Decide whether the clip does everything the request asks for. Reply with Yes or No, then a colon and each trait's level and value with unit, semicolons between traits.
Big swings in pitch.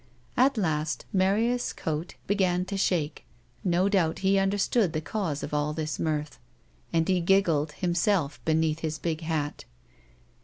No: average, 3.9 semitones